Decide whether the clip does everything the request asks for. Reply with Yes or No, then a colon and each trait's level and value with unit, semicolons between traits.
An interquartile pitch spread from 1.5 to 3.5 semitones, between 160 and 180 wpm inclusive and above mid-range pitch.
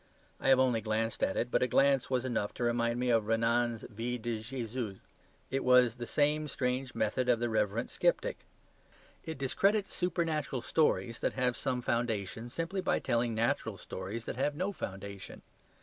No: average, 2.9 semitones; average, 175 wpm; low, 120 Hz